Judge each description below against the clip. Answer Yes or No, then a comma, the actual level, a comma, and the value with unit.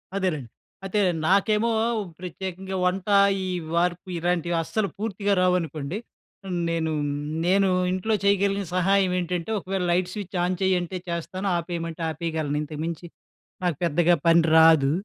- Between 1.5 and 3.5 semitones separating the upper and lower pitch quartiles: Yes, narrow, 2.5 semitones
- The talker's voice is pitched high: No, medium, 180 Hz